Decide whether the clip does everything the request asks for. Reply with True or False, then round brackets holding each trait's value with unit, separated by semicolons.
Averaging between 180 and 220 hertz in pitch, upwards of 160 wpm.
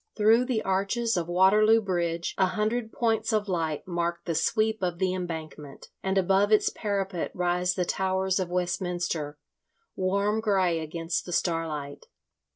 False (185 Hz; 150 wpm)